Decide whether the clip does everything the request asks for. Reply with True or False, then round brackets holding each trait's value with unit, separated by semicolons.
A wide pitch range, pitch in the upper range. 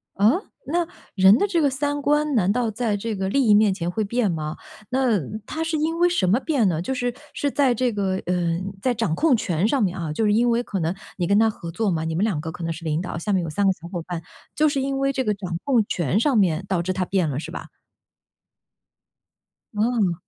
True (6.4 semitones; 210 Hz)